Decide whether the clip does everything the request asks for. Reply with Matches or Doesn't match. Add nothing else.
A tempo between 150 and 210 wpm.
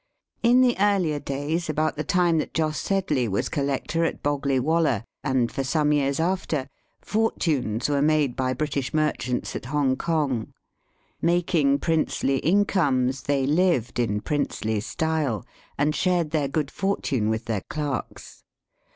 Doesn't match